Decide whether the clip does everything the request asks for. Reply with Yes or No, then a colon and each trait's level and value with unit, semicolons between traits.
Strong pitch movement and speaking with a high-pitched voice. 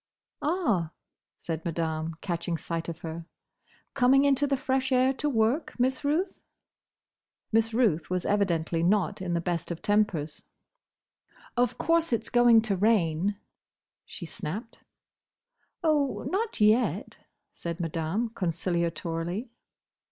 Yes: wide, 7.1 semitones; high, 205 Hz